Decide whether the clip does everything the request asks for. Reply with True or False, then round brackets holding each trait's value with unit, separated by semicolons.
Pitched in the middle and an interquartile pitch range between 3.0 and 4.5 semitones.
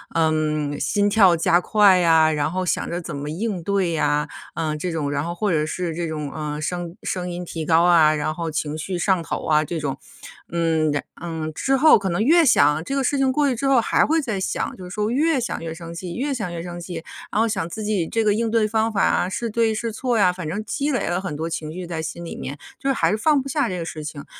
False (175 Hz; 5.3 semitones)